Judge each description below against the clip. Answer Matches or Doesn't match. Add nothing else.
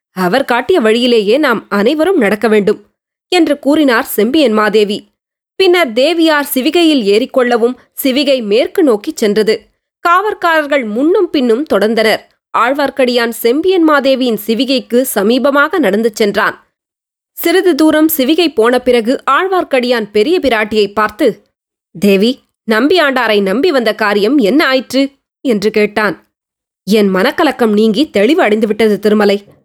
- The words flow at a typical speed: Matches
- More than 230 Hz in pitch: Matches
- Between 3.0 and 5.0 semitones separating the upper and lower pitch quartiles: Doesn't match